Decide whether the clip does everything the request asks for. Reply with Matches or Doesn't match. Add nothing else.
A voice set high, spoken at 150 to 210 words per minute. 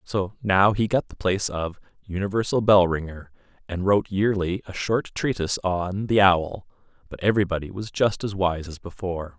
Doesn't match